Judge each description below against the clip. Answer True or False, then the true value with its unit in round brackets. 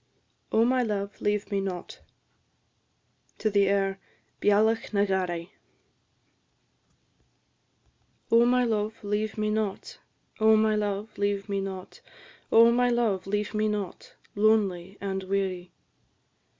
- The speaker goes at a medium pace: False (110 wpm)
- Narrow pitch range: True (1.9 semitones)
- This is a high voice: True (205 Hz)